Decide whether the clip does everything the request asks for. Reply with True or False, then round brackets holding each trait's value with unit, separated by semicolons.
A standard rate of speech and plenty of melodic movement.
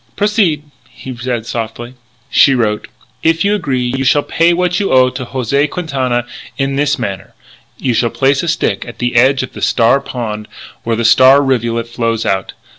False (185 wpm; 3.4 semitones)